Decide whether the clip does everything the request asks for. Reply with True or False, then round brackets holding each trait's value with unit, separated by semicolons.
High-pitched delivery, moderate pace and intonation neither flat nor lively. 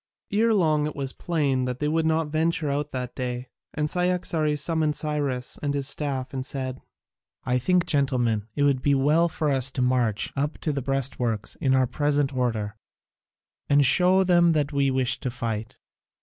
False (140 Hz; 180 wpm; 3.2 semitones)